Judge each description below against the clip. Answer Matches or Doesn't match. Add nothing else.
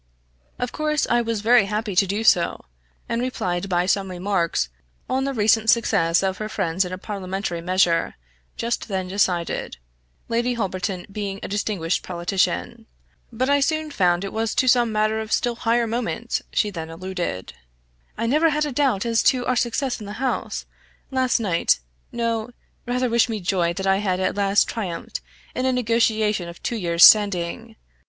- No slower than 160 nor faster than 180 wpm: Matches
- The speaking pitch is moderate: Doesn't match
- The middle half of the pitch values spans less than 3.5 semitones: Doesn't match